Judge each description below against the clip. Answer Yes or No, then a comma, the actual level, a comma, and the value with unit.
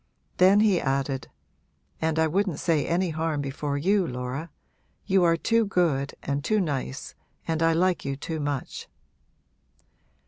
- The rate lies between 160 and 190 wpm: No, average, 145 wpm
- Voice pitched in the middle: Yes, medium, 160 Hz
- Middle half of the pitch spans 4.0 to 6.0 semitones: Yes, average, 4.4 semitones